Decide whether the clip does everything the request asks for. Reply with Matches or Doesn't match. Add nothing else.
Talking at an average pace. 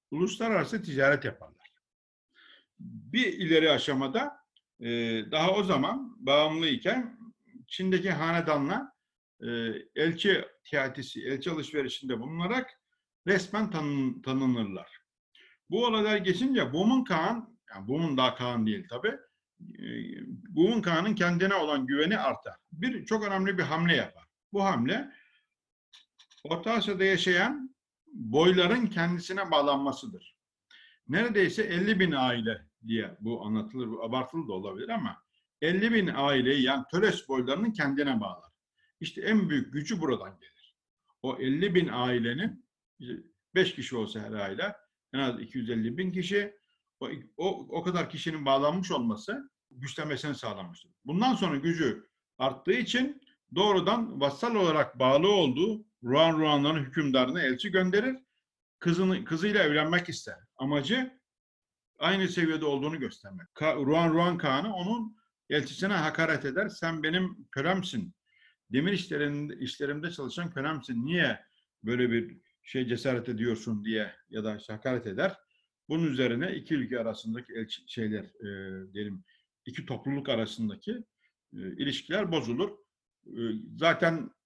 Matches